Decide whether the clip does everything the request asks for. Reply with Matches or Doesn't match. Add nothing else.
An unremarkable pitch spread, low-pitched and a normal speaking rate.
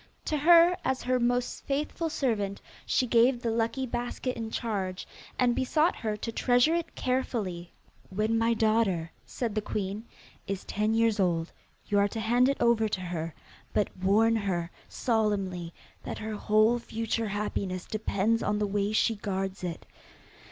Doesn't match